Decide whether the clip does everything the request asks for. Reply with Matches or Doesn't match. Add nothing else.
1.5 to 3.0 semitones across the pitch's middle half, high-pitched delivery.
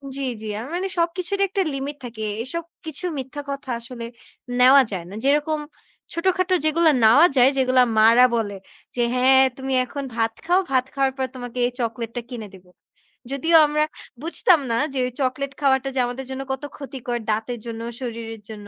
Doesn't match